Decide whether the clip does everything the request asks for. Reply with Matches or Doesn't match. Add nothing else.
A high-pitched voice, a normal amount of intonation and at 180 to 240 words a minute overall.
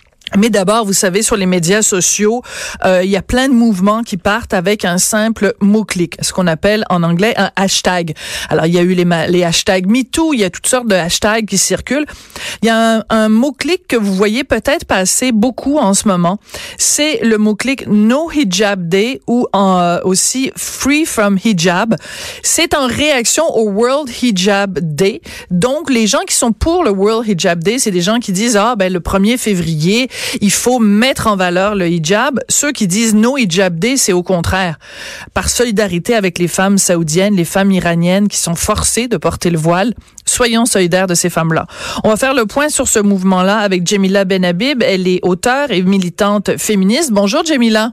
Matches